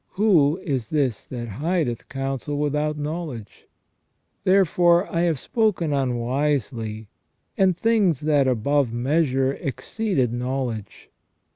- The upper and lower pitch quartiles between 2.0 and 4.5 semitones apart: No, average, 5.0 semitones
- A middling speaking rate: No, slow, 110 wpm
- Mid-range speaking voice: Yes, medium, 145 Hz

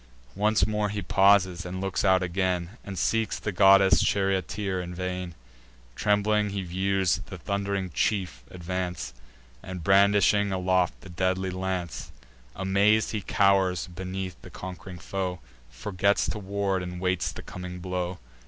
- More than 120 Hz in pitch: No, very low, 95 Hz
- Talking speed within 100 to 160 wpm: Yes, average, 140 wpm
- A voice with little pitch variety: Yes, narrow, 1.6 semitones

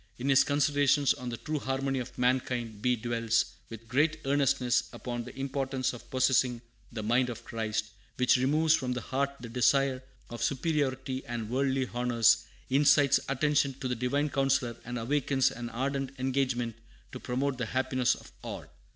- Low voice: Yes, low, 130 Hz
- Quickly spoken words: No, average, 165 wpm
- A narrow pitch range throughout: Yes, narrow, 2.2 semitones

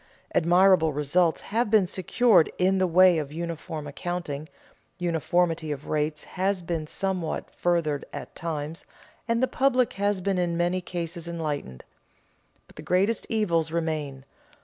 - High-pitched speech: No, medium, 170 Hz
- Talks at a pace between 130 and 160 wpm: Yes, average, 140 wpm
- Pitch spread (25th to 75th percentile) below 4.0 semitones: Yes, average, 3.1 semitones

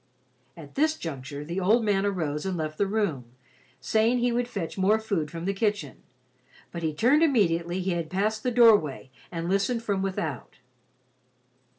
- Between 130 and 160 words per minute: No, average, 170 wpm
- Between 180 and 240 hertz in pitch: Yes, high, 190 Hz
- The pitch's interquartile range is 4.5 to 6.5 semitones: Yes, average, 5.2 semitones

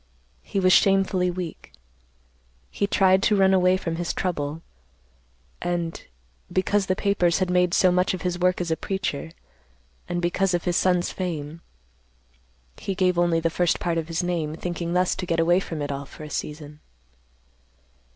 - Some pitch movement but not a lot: No, narrow, 2.0 semitones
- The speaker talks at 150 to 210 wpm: Yes, average, 170 wpm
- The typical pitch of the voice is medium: Yes, medium, 175 Hz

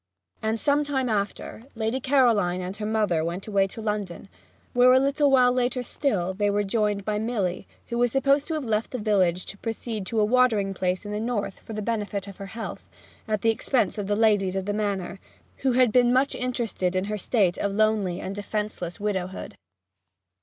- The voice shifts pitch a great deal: No, average, 3.7 semitones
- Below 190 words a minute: No, fast, 205 wpm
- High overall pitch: Yes, high, 215 Hz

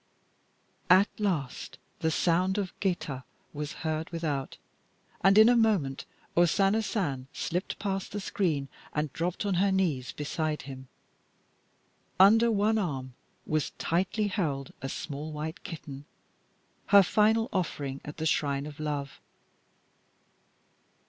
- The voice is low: No, medium, 165 Hz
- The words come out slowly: Yes, slow, 130 wpm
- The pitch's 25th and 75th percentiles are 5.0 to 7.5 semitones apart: Yes, average, 5.3 semitones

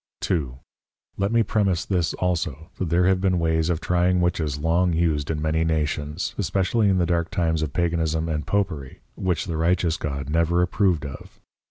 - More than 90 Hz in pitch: No, very low, 85 Hz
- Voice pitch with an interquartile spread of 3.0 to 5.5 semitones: No, narrow, 2.6 semitones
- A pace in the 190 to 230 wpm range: No, average, 180 wpm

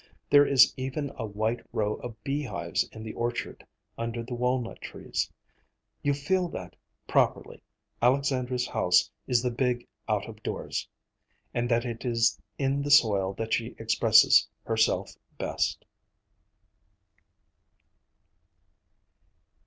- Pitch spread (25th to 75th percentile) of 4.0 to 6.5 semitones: No, average, 2.9 semitones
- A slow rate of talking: Yes, slow, 120 wpm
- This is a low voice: Yes, low, 120 Hz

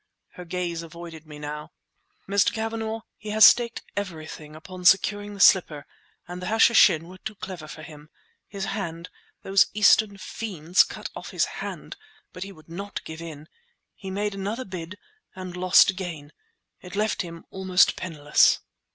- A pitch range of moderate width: Yes, average, 3.7 semitones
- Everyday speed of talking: Yes, average, 150 wpm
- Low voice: No, medium, 185 Hz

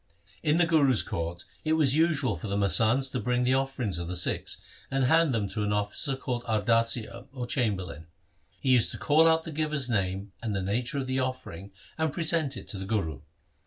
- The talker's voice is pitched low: Yes, low, 125 Hz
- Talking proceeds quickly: Yes, fast, 210 wpm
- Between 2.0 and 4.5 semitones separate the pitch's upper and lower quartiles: No, wide, 5.5 semitones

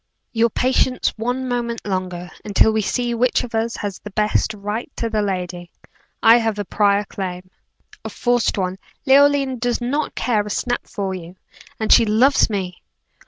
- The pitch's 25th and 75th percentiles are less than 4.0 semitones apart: Yes, average, 3.6 semitones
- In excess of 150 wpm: Yes, average, 170 wpm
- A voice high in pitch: Yes, high, 220 Hz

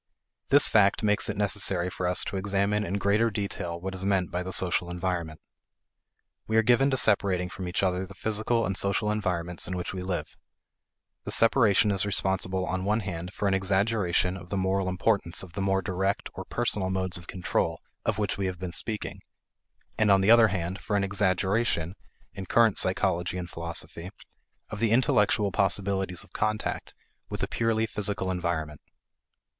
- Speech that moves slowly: No, average, 180 wpm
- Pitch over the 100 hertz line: No, very low, 95 Hz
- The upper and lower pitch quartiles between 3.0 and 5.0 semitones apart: No, narrow, 2.4 semitones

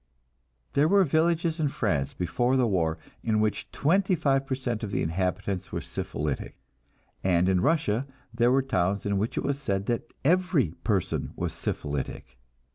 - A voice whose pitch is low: Yes, low, 115 Hz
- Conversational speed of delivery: Yes, average, 165 wpm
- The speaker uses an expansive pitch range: Yes, wide, 7.1 semitones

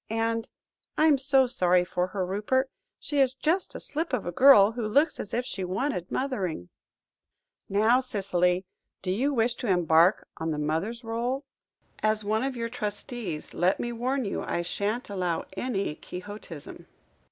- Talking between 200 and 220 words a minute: No, average, 165 wpm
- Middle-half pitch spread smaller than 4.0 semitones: No, wide, 5.6 semitones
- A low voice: No, high, 215 Hz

